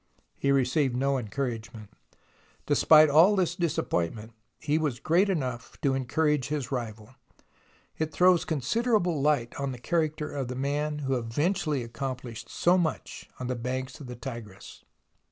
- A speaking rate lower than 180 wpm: Yes, average, 145 wpm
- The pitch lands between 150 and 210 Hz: No, medium, 140 Hz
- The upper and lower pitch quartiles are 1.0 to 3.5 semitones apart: No, average, 4.2 semitones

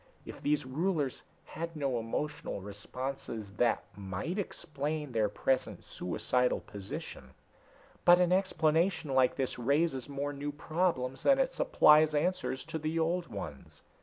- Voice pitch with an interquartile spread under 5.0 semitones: Yes, average, 4.6 semitones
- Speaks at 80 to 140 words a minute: Yes, slow, 135 wpm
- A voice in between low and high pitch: Yes, medium, 145 Hz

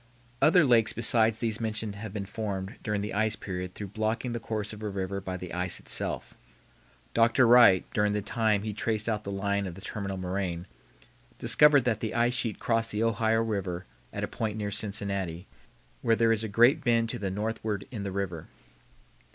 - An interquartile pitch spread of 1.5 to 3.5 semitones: Yes, narrow, 2.5 semitones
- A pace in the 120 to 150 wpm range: No, average, 195 wpm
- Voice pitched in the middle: No, low, 105 Hz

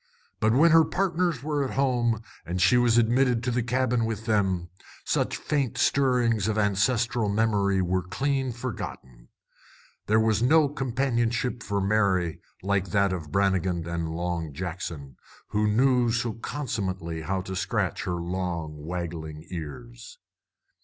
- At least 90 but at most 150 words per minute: Yes, average, 140 wpm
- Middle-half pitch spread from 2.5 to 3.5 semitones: No, wide, 5.4 semitones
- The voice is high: No, low, 105 Hz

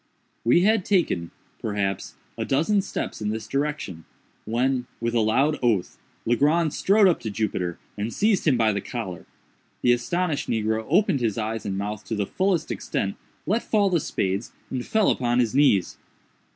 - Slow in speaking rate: No, average, 170 wpm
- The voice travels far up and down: Yes, wide, 7.1 semitones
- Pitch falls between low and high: No, low, 120 Hz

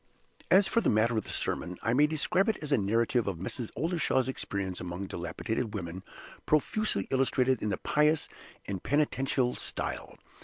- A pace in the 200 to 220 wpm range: No, average, 165 wpm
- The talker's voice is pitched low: Yes, low, 120 Hz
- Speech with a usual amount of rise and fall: No, wide, 7.1 semitones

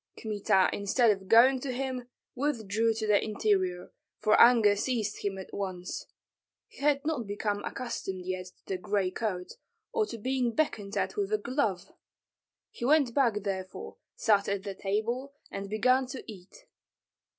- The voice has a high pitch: Yes, high, 215 Hz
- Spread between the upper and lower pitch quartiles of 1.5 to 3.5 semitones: No, average, 4.3 semitones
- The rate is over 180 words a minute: No, average, 160 wpm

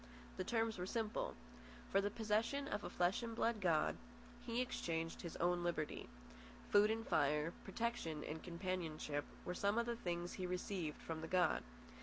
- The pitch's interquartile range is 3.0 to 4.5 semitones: No, average, 5.1 semitones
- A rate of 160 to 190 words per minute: Yes, average, 170 wpm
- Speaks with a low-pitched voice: No, medium, 185 Hz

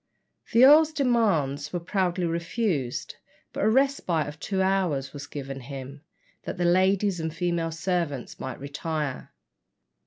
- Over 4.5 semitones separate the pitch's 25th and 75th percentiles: Yes, average, 5.2 semitones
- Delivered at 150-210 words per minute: No, slow, 135 wpm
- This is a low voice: No, medium, 170 Hz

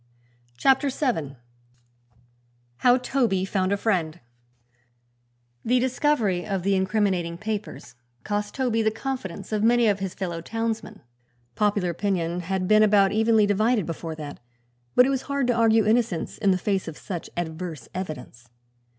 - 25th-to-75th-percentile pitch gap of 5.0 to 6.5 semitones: No, average, 4.2 semitones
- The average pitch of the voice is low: No, high, 205 Hz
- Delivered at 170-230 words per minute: No, average, 145 wpm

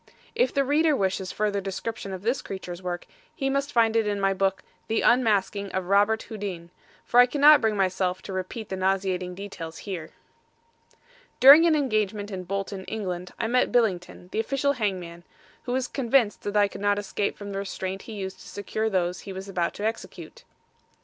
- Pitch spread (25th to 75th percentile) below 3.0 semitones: No, average, 3.3 semitones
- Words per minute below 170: No, average, 190 wpm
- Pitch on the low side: No, high, 200 Hz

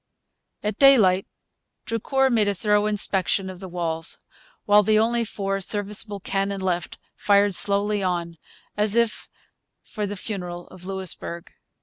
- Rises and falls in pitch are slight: Yes, narrow, 2.2 semitones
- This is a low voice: No, high, 200 Hz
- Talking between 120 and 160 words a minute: Yes, slow, 135 wpm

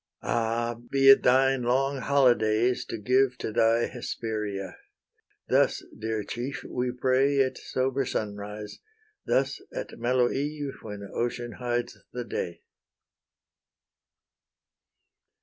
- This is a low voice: Yes, low, 120 Hz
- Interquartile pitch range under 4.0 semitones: Yes, average, 3.1 semitones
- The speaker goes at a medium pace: No, slow, 110 wpm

